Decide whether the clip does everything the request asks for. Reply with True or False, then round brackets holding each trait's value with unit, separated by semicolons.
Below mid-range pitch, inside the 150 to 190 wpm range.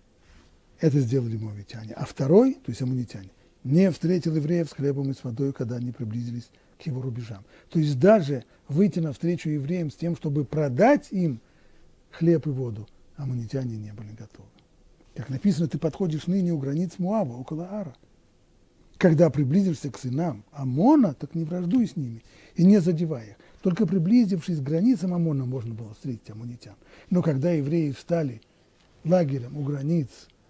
False (150 Hz; 155 wpm)